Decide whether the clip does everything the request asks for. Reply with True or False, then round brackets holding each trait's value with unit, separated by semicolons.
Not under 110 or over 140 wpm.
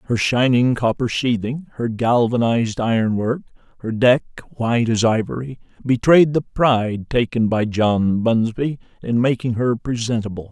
True (135 wpm)